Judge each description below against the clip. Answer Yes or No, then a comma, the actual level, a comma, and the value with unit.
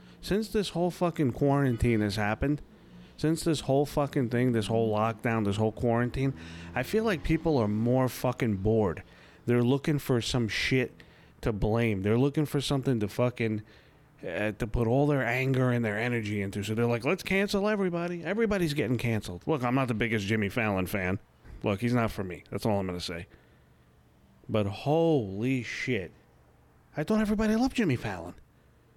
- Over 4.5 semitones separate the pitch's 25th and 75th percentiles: Yes, wide, 5.6 semitones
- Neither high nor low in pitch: No, low, 120 Hz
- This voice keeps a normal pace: Yes, average, 180 wpm